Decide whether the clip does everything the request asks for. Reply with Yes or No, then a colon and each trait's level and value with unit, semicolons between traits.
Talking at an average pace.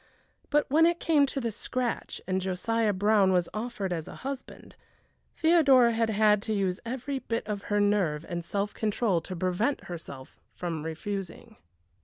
Yes: average, 165 wpm